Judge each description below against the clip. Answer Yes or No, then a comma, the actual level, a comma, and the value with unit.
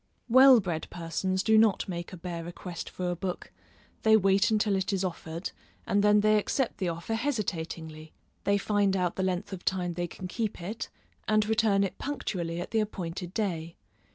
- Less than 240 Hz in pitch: Yes, high, 190 Hz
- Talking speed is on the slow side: No, average, 185 wpm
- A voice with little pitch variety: No, average, 3.5 semitones